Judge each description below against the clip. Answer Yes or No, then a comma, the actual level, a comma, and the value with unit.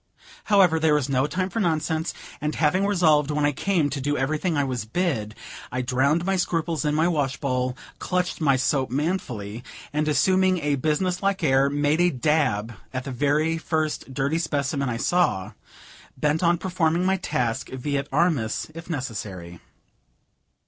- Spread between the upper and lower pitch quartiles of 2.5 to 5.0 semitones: Yes, average, 4.3 semitones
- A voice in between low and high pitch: Yes, medium, 150 Hz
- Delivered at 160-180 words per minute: Yes, average, 165 wpm